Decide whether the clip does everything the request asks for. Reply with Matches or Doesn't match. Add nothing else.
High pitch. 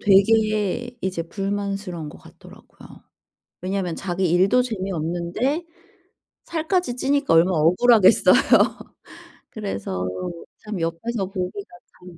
Matches